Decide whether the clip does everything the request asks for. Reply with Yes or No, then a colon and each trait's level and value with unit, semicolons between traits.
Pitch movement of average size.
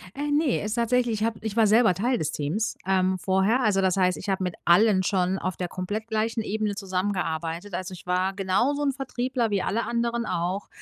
Yes: average, 3.9 semitones